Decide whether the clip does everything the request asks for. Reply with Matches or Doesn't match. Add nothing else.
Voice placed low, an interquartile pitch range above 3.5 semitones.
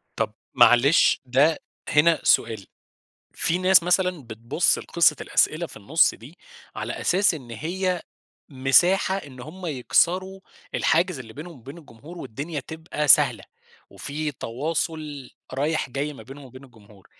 Doesn't match